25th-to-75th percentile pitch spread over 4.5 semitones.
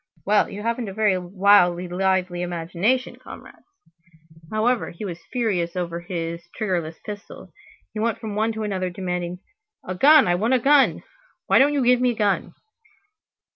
No: average, 4.2 semitones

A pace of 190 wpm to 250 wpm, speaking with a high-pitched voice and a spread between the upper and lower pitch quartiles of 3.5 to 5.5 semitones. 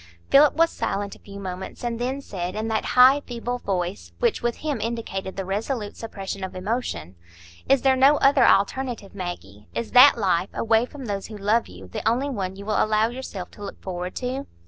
Yes: average, 200 wpm; high, 215 Hz; average, 4.7 semitones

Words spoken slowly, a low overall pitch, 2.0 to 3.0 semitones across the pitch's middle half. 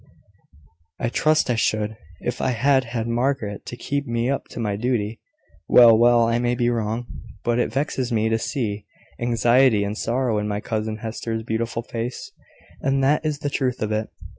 No: average, 185 wpm; low, 120 Hz; narrow, 2.4 semitones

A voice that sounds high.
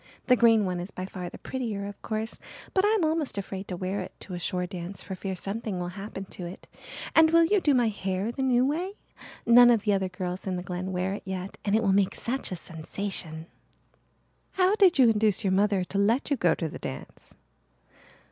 Yes: high, 200 Hz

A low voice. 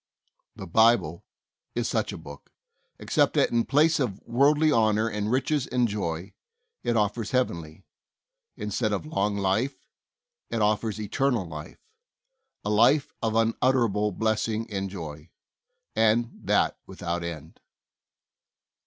Yes: low, 110 Hz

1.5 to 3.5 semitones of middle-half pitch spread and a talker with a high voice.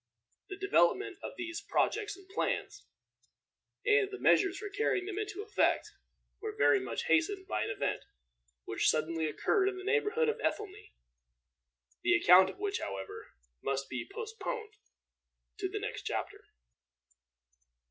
Yes: average, 3.0 semitones; very high, 395 Hz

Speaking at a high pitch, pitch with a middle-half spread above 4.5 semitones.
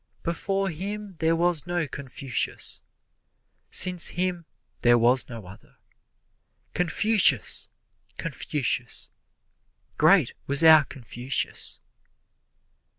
No: medium, 165 Hz; average, 5.3 semitones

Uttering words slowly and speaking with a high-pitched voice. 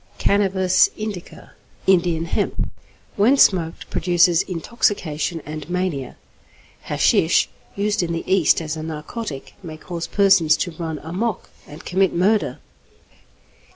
No: slow, 120 wpm; medium, 175 Hz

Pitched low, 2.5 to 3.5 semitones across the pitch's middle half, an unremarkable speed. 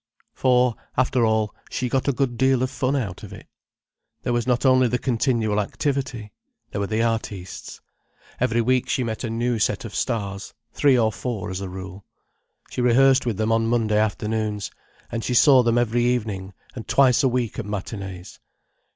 Yes: low, 115 Hz; average, 3.0 semitones; average, 180 wpm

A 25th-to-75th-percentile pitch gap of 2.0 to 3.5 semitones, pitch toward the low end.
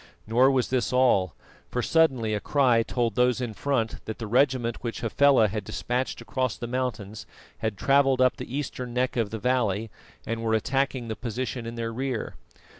Yes: narrow, 2.5 semitones; low, 120 Hz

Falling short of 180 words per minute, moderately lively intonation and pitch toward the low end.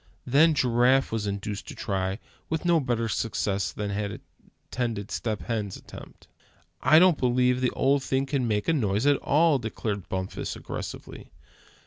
Yes: average, 160 wpm; average, 4.9 semitones; low, 120 Hz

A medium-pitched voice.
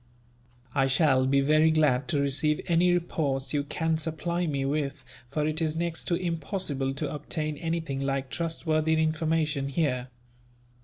Yes: medium, 155 Hz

